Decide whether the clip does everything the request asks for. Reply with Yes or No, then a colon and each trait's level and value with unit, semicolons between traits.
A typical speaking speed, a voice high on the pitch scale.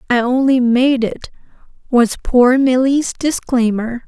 No: slow, 120 wpm; very high, 250 Hz